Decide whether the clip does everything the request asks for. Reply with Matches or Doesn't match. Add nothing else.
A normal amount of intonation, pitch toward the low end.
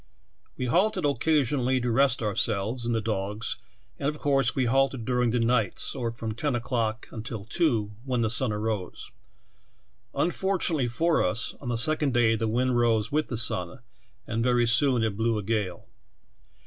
Matches